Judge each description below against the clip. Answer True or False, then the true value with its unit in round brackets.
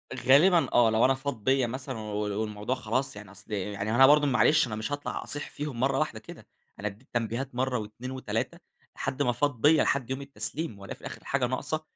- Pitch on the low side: True (125 Hz)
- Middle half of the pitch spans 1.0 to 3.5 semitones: False (4.1 semitones)